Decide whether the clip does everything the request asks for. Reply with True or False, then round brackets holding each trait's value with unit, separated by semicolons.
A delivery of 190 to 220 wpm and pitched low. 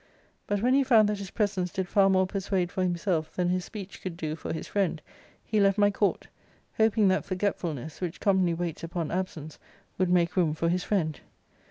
False (200 wpm; 185 Hz)